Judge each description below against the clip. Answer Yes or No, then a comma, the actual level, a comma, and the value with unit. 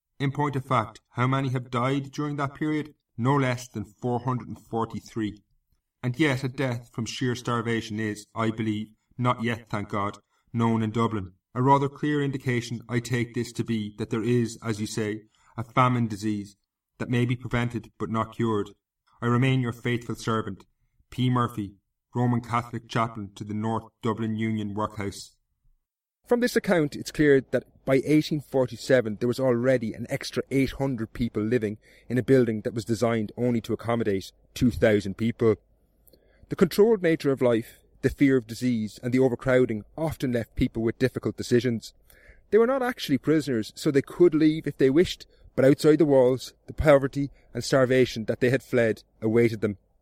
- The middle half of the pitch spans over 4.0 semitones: No, average, 3.2 semitones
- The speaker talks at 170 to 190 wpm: Yes, average, 180 wpm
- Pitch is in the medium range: No, low, 120 Hz